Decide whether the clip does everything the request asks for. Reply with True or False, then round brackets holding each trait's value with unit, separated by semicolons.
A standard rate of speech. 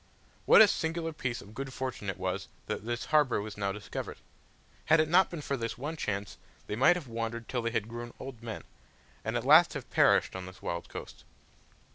False (210 wpm)